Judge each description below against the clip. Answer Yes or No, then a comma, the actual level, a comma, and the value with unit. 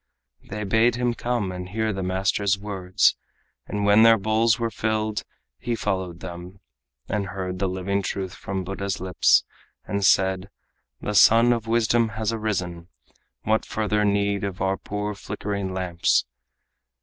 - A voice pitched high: No, low, 100 Hz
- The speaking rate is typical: Yes, average, 150 wpm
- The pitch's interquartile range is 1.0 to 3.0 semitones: Yes, narrow, 2.6 semitones